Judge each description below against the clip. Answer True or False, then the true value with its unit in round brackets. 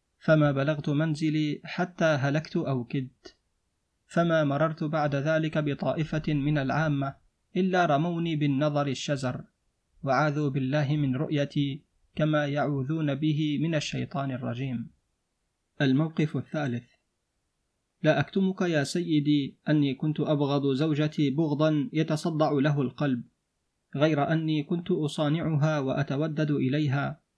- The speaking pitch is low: False (150 Hz)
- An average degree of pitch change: False (2.0 semitones)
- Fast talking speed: False (105 wpm)